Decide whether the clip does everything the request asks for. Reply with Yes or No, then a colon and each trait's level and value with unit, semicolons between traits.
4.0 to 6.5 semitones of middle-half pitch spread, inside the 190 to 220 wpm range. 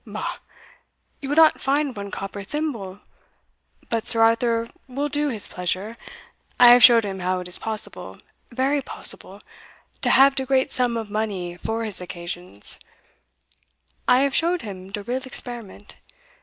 No: average, 5.0 semitones; average, 155 wpm